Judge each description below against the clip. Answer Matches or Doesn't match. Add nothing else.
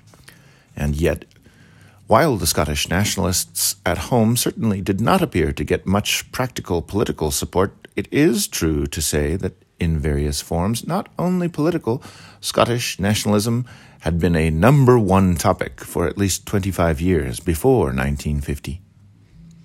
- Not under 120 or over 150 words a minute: Matches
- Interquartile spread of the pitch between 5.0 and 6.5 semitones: Matches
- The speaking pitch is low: Matches